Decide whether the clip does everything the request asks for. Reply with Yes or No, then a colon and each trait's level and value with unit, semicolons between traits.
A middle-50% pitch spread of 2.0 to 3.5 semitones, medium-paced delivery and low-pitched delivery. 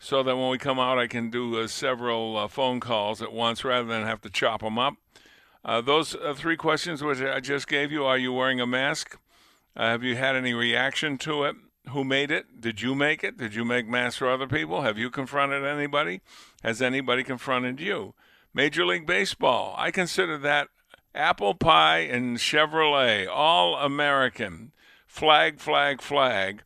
Yes: average, 2.9 semitones; average, 185 wpm; low, 130 Hz